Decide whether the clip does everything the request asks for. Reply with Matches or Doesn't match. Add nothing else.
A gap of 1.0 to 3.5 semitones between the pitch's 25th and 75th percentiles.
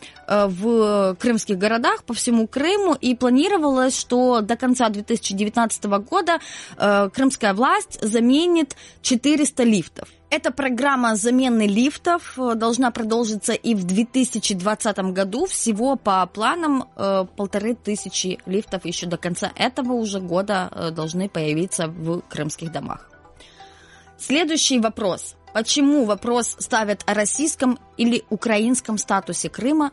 Doesn't match